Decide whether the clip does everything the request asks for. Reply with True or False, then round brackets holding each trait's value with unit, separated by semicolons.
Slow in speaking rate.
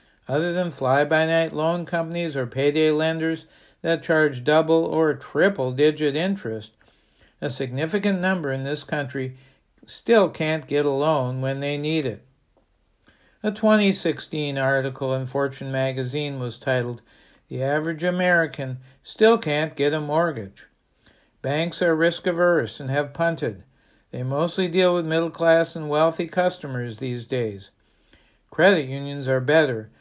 True (130 wpm)